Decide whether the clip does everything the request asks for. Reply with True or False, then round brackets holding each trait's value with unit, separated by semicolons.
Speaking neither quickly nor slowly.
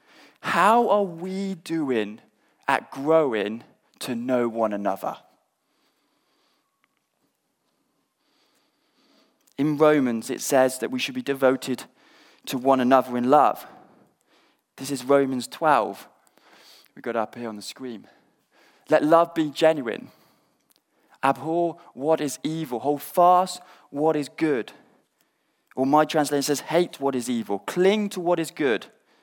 False (125 wpm)